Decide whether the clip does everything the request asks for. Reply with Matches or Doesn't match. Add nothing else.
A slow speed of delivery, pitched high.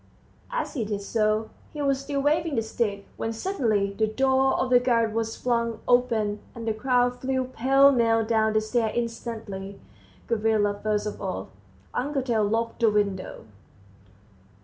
Doesn't match